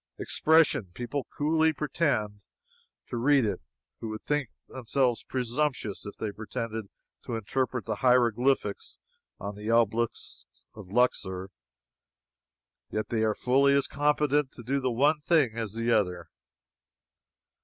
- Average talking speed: No, slow, 130 wpm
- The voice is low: Yes, low, 120 Hz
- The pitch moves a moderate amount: Yes, average, 4.3 semitones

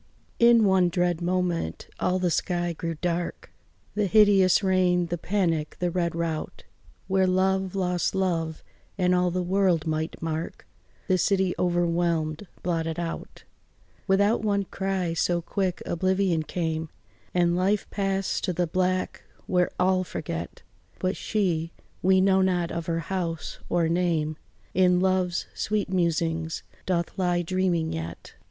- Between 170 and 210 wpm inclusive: No, average, 140 wpm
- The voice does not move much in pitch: Yes, narrow, 2.0 semitones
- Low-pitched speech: No, medium, 180 Hz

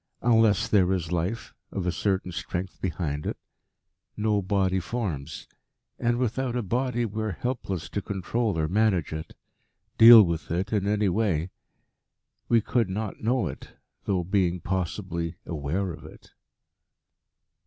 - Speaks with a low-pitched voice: Yes, very low, 95 Hz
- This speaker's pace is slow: No, average, 145 wpm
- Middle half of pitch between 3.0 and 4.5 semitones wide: Yes, average, 4.2 semitones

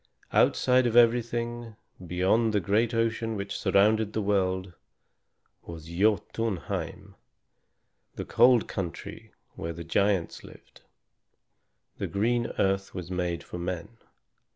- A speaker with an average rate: No, slow, 110 wpm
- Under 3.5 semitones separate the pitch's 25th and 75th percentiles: No, average, 3.9 semitones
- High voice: No, low, 105 Hz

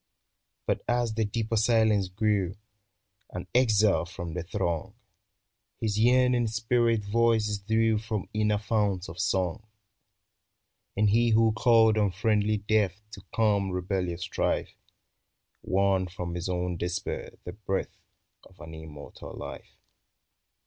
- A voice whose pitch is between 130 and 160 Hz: No, low, 105 Hz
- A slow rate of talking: Yes, slow, 125 wpm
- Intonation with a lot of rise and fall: No, average, 3.3 semitones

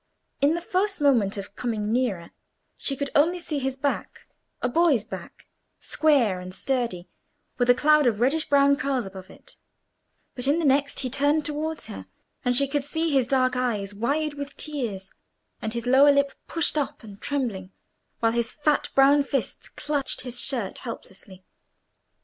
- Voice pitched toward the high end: Yes, very high, 270 Hz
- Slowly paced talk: No, average, 165 wpm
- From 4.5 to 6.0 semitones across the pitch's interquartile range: No, average, 4.1 semitones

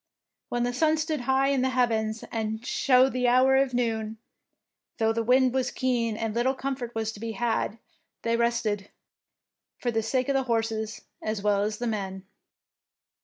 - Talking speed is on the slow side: No, average, 175 wpm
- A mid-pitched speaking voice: No, high, 235 Hz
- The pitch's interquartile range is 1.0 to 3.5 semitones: Yes, average, 2.7 semitones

